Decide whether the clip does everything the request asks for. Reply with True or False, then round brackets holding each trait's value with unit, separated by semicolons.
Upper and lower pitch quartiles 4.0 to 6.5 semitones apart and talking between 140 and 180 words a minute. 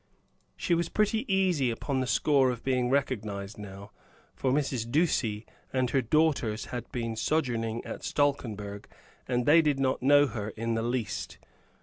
True (4.3 semitones; 155 wpm)